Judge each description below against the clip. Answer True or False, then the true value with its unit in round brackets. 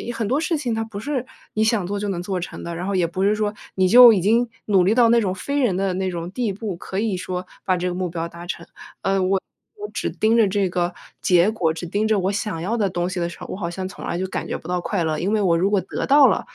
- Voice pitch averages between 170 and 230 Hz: True (190 Hz)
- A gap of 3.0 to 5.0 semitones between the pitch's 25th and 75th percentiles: True (3.4 semitones)